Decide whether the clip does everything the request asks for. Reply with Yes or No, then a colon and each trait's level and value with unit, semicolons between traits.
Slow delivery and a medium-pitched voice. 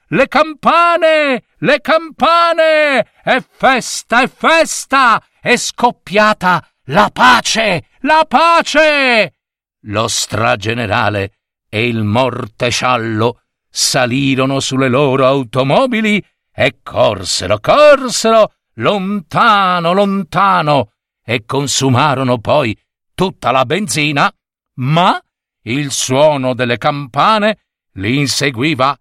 Yes: slow, 85 wpm; medium, 155 Hz